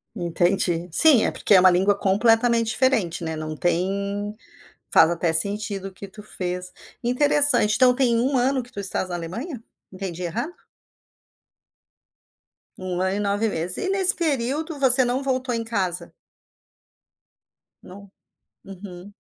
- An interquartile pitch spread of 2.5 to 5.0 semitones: No, wide, 5.4 semitones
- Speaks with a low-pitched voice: No, high, 205 Hz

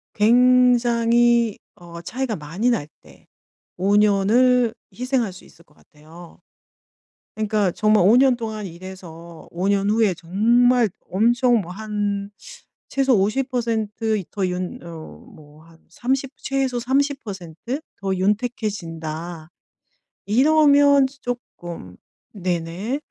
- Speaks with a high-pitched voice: Yes, high, 210 Hz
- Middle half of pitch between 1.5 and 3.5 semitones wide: No, wide, 5.6 semitones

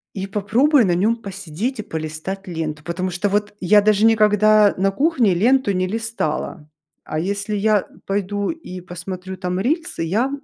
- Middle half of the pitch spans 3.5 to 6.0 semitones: No, average, 2.9 semitones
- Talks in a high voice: Yes, high, 200 Hz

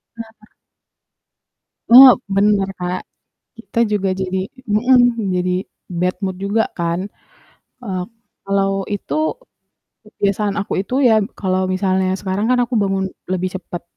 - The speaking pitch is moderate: No, high, 195 Hz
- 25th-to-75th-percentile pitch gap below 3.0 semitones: Yes, narrow, 2.4 semitones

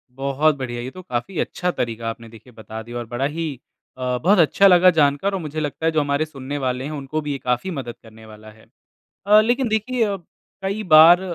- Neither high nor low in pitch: Yes, medium, 145 Hz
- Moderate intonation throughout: No, wide, 6.4 semitones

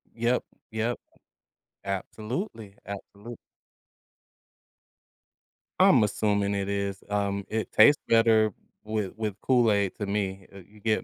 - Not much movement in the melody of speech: Yes, narrow, 2.0 semitones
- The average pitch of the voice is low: Yes, low, 105 Hz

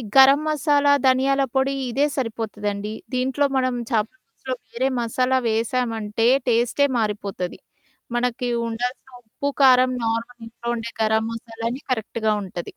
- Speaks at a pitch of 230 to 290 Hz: Yes, high, 235 Hz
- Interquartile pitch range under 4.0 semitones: Yes, average, 2.8 semitones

